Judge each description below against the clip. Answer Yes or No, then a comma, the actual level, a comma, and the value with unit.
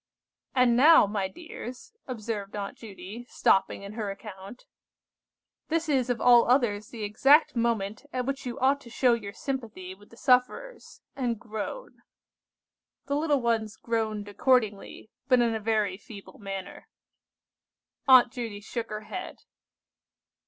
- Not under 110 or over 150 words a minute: Yes, average, 140 wpm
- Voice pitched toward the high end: Yes, high, 230 Hz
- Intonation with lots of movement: No, average, 3.7 semitones